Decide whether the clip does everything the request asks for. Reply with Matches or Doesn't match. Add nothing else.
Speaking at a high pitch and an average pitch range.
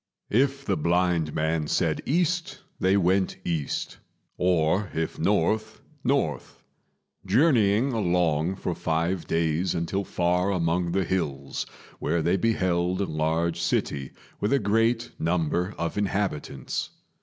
Doesn't match